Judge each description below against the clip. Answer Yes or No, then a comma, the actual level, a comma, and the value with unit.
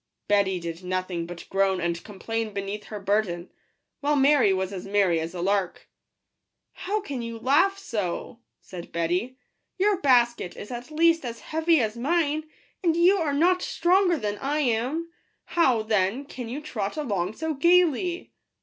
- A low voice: No, high, 235 Hz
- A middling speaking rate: Yes, average, 175 wpm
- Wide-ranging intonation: Yes, wide, 8.1 semitones